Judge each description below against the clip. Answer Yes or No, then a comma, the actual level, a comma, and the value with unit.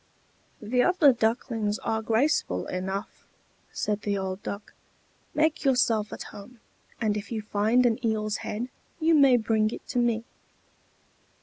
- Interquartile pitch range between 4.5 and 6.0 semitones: No, average, 2.9 semitones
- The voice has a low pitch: No, high, 220 Hz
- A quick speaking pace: No, average, 140 wpm